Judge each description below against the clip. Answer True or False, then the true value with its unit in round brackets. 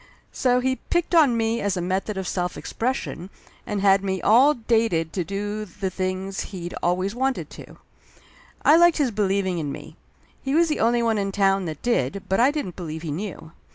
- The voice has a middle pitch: False (200 Hz)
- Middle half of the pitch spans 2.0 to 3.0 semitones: False (4.5 semitones)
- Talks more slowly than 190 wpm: False (195 wpm)